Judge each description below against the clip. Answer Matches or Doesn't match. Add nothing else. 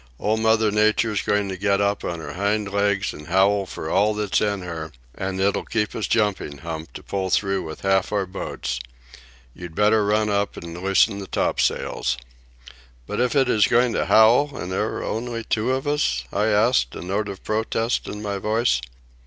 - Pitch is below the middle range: Matches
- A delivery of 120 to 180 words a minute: Doesn't match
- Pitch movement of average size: Doesn't match